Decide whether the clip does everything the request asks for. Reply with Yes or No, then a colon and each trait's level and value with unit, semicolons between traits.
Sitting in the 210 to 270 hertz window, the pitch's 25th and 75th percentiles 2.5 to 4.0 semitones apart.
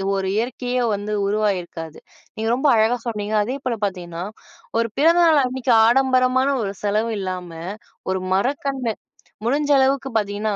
No: high, 230 Hz; average, 4.5 semitones